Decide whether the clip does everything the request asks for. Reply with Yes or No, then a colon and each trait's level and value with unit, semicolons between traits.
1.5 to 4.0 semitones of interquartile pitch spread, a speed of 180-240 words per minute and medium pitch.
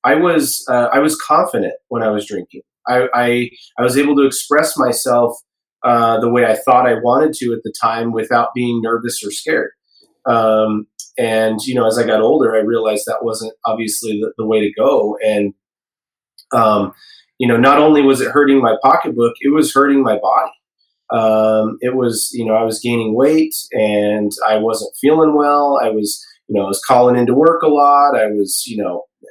No: average, 3.1 semitones; average, 200 wpm; low, 115 Hz